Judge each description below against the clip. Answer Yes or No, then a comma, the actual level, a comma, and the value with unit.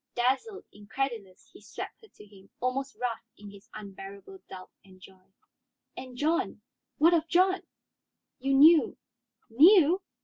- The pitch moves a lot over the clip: Yes, wide, 8.1 semitones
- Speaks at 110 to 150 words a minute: Yes, average, 140 wpm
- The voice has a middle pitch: No, very high, 255 Hz